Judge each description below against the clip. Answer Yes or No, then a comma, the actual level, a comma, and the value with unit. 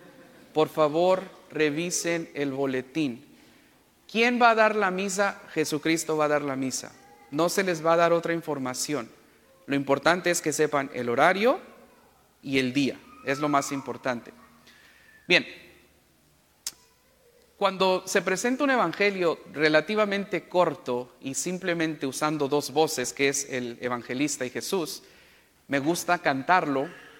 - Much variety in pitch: No, average, 4.5 semitones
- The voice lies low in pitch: No, medium, 155 Hz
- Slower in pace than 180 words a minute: Yes, slow, 135 wpm